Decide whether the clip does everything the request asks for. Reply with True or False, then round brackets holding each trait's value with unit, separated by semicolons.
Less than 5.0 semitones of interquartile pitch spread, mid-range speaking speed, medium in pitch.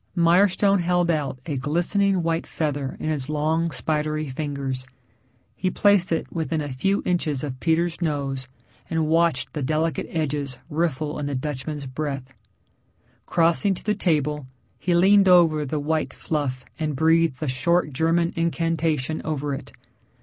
True (2.7 semitones; 150 wpm; 155 Hz)